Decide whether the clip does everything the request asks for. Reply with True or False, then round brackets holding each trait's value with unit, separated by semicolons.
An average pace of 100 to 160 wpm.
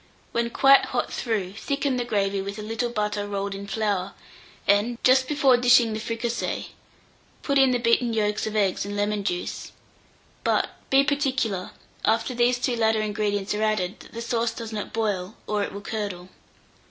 False (180 wpm)